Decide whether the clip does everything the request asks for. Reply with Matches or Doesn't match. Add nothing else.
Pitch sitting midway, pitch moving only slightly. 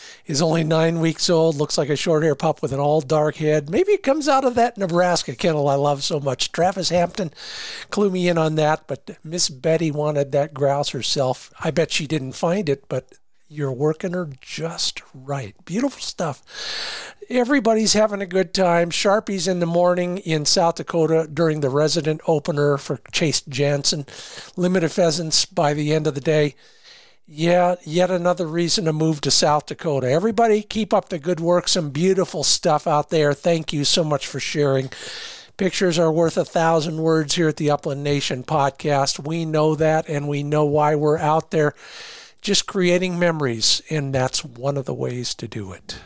Doesn't match